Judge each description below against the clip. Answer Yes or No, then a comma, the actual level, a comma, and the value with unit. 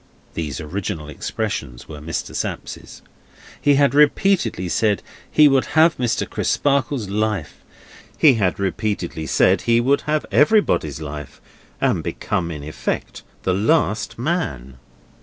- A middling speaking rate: No, slow, 125 wpm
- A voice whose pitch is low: Yes, low, 105 Hz